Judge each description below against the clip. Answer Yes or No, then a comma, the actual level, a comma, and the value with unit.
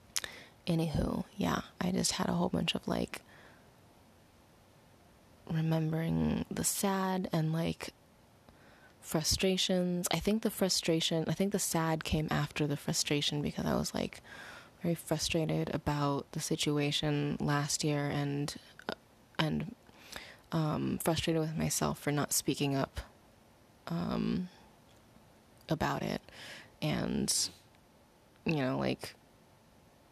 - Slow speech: Yes, slow, 110 wpm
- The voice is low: No, medium, 155 Hz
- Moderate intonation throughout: Yes, average, 3.0 semitones